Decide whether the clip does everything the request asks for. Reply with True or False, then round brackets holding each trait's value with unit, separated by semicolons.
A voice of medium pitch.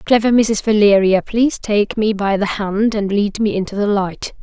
False (210 Hz)